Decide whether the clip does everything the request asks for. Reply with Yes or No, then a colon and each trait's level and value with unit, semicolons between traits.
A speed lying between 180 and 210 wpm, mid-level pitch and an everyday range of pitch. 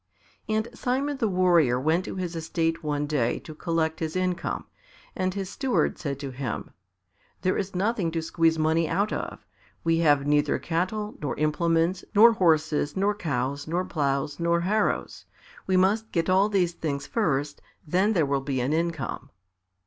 No: average, 165 wpm; medium, 165 Hz; average, 4.0 semitones